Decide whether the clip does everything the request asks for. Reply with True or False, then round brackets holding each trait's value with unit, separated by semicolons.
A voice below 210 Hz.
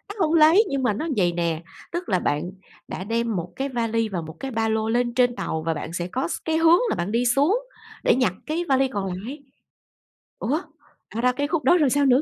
False (240 Hz)